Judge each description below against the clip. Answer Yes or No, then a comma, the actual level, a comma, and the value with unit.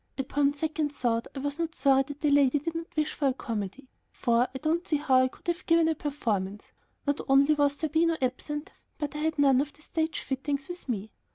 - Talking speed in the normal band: No, fast, 220 wpm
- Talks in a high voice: Yes, very high, 285 Hz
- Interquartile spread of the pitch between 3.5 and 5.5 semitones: No, average, 2.8 semitones